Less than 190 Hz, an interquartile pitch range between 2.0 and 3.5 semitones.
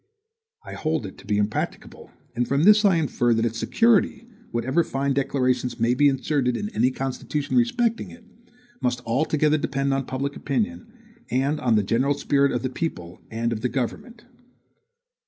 No: low, 135 Hz; average, 4.3 semitones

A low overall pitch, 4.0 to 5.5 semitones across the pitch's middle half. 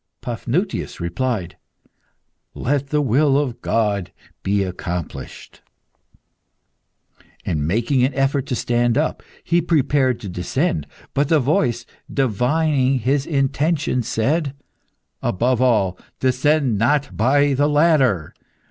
Yes: low, 130 Hz; average, 4.3 semitones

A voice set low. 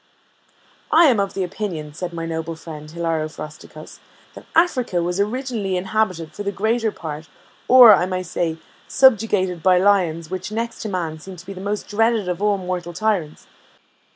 No: medium, 185 Hz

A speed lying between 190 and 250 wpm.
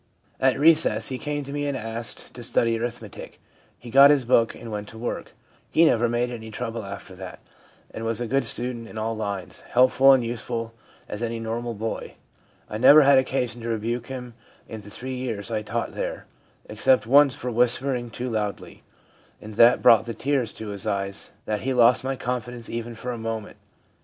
Yes: average, 195 wpm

